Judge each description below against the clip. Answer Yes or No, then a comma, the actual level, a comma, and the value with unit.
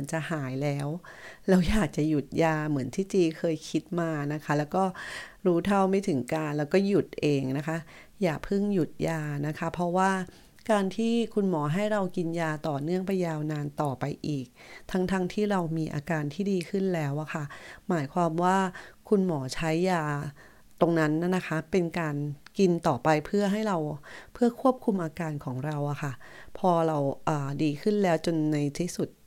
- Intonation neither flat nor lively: Yes, average, 3.8 semitones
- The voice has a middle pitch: Yes, medium, 165 Hz